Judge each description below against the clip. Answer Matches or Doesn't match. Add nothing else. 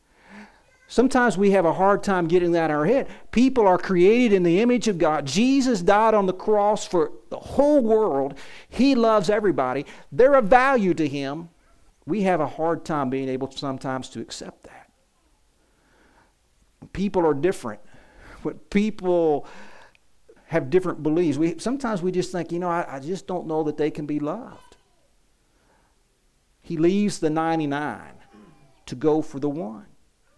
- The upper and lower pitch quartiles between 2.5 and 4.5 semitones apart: Doesn't match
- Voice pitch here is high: Doesn't match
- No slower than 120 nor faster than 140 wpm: Doesn't match